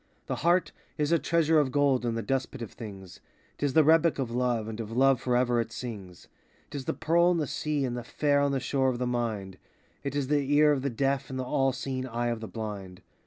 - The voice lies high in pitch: No, low, 130 Hz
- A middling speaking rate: No, fast, 255 wpm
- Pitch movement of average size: Yes, average, 3.5 semitones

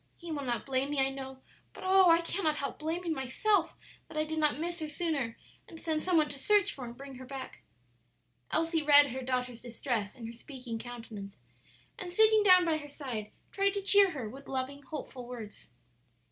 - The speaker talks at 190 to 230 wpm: Yes, average, 200 wpm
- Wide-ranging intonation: No, average, 4.8 semitones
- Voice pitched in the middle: No, very high, 285 Hz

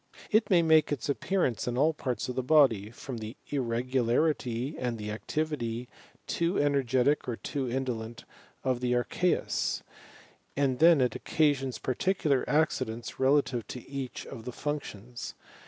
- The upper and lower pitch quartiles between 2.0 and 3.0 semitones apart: No, average, 3.6 semitones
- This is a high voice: No, low, 130 Hz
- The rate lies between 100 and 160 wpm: Yes, average, 150 wpm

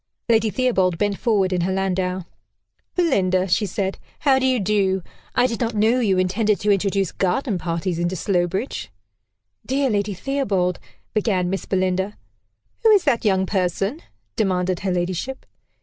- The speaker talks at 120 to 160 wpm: Yes, average, 150 wpm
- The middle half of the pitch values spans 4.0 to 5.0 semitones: No, average, 3.5 semitones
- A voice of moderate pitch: No, high, 195 Hz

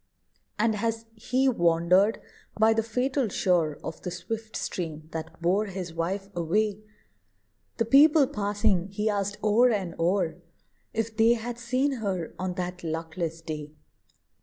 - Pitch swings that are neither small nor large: Yes, average, 4.8 semitones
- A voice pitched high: Yes, high, 200 Hz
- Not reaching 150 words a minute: Yes, average, 140 wpm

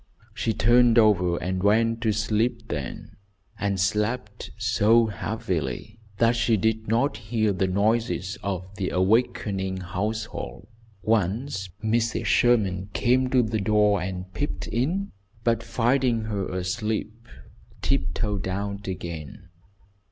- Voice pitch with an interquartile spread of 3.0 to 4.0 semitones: Yes, average, 3.3 semitones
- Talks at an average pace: No, slow, 120 wpm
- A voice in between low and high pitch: No, low, 105 Hz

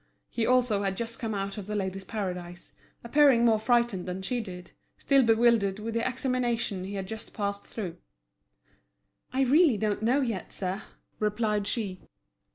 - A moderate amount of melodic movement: Yes, average, 3.4 semitones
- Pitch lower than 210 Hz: No, high, 215 Hz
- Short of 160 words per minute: No, average, 165 wpm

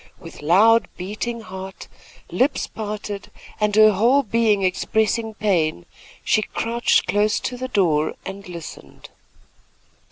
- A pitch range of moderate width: Yes, average, 3.2 semitones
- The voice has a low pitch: No, high, 210 Hz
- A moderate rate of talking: No, slow, 120 wpm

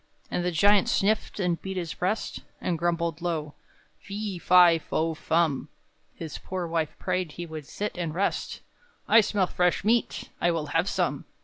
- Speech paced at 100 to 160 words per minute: No, average, 170 wpm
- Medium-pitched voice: Yes, medium, 175 Hz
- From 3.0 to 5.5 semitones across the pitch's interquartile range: No, narrow, 2.6 semitones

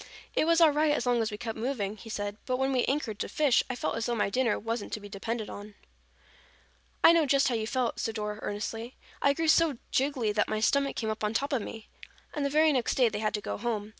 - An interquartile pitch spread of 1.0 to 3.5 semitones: No, average, 4.5 semitones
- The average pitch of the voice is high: Yes, high, 235 Hz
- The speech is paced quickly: Yes, fast, 260 wpm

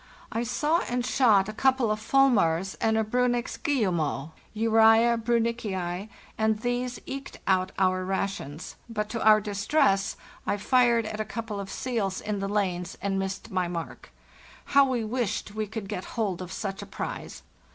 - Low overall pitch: No, high, 215 Hz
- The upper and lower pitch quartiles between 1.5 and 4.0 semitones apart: Yes, average, 3.7 semitones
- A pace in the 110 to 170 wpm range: Yes, average, 160 wpm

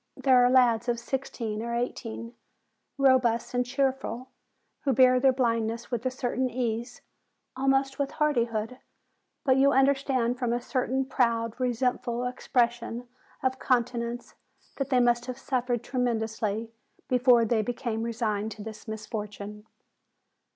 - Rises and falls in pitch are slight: Yes, narrow, 2.0 semitones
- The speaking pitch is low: No, high, 245 Hz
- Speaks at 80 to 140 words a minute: Yes, slow, 135 wpm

